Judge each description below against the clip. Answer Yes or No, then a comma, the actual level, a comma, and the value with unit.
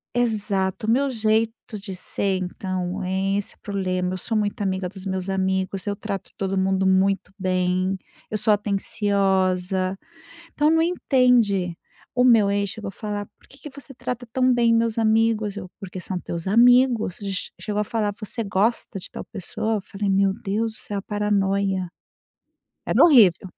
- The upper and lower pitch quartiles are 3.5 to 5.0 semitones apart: No, average, 2.8 semitones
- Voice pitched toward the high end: Yes, high, 200 Hz